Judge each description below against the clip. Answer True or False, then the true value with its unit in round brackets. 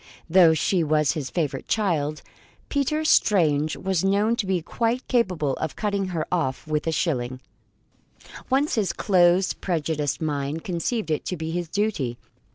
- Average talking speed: True (155 wpm)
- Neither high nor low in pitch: True (170 Hz)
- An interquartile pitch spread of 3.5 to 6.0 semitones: True (4.6 semitones)